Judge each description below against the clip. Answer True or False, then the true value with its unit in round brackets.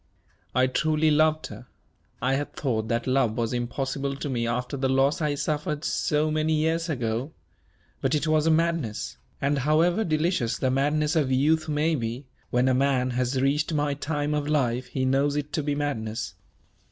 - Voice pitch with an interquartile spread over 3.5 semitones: False (3.1 semitones)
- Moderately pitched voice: True (145 Hz)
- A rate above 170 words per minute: True (180 wpm)